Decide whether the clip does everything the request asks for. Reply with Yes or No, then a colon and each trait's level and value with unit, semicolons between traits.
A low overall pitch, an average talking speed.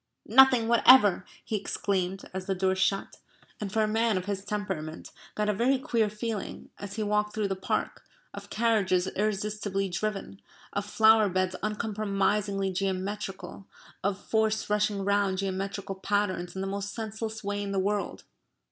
No: high, 205 Hz; average, 155 wpm